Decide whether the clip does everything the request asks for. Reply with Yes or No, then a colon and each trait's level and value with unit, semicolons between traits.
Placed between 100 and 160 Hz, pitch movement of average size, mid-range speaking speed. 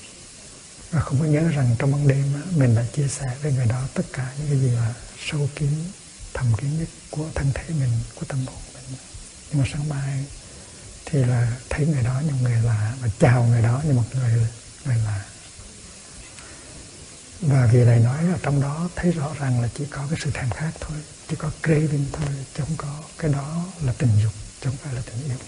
Yes: low, 135 Hz; average, 3.8 semitones; average, 215 wpm